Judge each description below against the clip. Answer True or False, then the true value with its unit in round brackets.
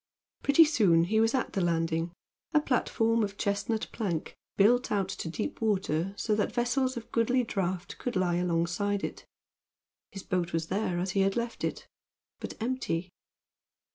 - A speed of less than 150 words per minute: False (165 wpm)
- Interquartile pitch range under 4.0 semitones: False (4.7 semitones)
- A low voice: False (200 Hz)